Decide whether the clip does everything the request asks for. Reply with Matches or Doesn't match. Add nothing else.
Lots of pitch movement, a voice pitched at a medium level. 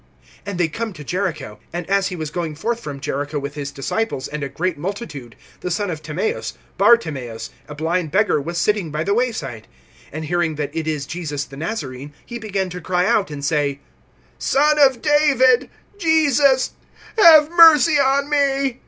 Matches